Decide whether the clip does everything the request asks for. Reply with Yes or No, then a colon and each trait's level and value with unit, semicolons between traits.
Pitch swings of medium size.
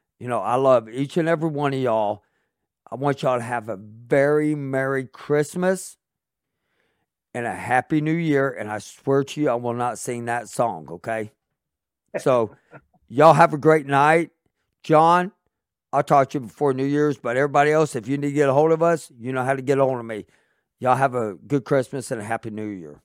Yes: average, 3.9 semitones